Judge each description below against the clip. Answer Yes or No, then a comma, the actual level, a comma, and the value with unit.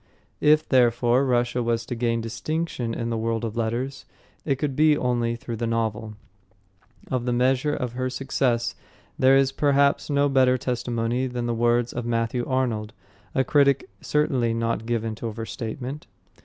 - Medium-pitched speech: No, low, 120 Hz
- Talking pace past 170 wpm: No, average, 160 wpm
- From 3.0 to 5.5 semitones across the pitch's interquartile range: No, narrow, 2.4 semitones